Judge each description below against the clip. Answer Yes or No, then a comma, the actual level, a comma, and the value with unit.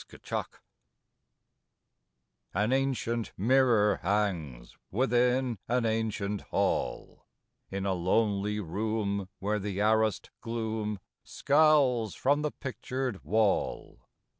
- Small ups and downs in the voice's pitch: No, average, 3.6 semitones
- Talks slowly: Yes, slow, 95 wpm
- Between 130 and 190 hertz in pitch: No, low, 110 Hz